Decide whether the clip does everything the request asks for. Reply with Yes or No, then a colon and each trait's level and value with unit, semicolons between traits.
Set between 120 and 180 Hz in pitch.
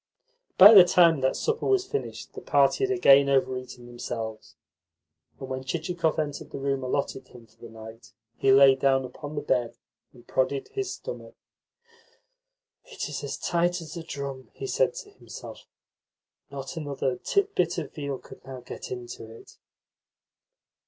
Yes: medium, 140 Hz